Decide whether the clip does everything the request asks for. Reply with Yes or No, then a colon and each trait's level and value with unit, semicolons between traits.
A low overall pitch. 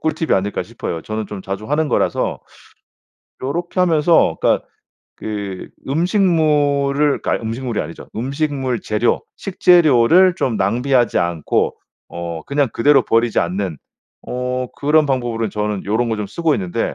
Yes: low, 125 Hz